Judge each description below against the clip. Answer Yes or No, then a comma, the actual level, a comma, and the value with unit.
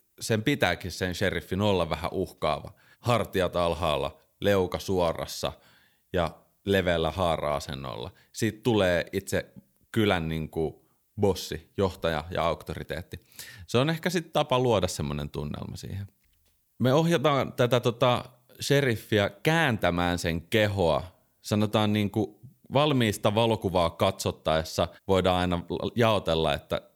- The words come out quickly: No, average, 115 wpm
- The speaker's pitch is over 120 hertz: No, low, 100 Hz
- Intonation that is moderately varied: No, wide, 5.7 semitones